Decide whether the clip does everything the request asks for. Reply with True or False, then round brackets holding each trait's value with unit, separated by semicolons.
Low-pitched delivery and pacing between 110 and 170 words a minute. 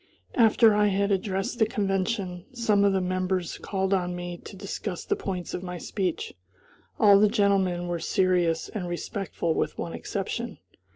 False (190 Hz; 165 wpm)